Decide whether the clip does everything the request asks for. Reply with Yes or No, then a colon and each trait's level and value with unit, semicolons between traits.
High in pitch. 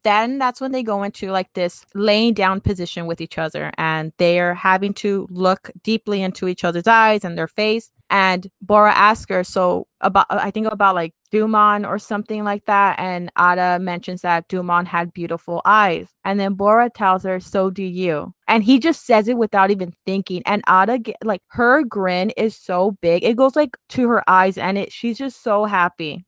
Yes: high, 195 Hz